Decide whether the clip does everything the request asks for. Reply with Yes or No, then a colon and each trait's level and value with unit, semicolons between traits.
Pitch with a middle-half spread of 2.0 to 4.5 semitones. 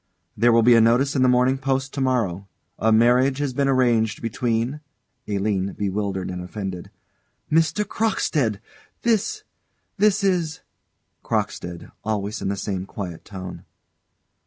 No: average, 5.3 semitones